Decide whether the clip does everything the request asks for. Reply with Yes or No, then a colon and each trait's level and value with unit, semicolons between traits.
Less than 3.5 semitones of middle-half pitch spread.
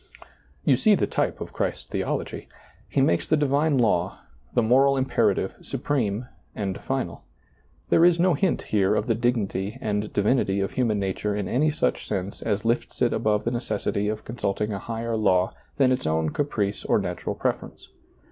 No: average, 4.7 semitones